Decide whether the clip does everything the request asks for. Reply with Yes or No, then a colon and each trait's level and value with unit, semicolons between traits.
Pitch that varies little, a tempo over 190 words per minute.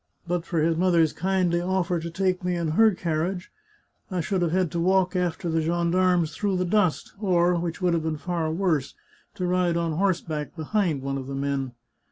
Yes: narrow, 2.2 semitones; average, 200 wpm